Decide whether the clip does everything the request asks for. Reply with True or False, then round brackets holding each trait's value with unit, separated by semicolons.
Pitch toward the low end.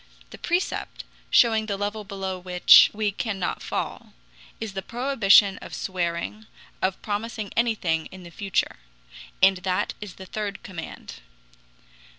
False (200 Hz)